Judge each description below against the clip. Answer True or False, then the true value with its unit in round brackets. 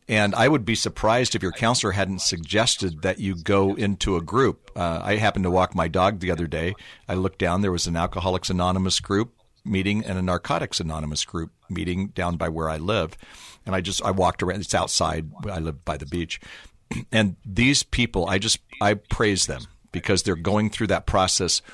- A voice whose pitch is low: True (95 Hz)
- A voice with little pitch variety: False (3.1 semitones)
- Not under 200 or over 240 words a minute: True (205 wpm)